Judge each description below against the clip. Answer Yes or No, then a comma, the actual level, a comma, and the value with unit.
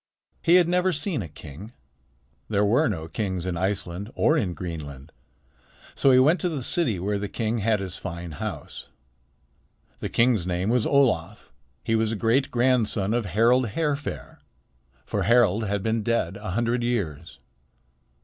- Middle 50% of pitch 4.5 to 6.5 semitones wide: Yes, average, 4.9 semitones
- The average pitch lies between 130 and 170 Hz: No, low, 110 Hz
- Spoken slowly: No, average, 160 wpm